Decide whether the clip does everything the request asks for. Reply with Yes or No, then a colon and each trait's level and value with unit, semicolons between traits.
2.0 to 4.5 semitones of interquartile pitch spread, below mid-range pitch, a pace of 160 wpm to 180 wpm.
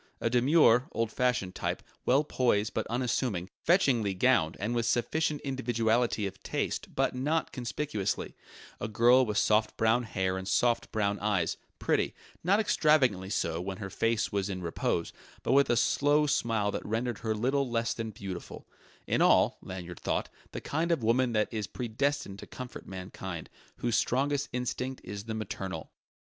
Yes: average, 4.1 semitones; low, 115 Hz; average, 165 wpm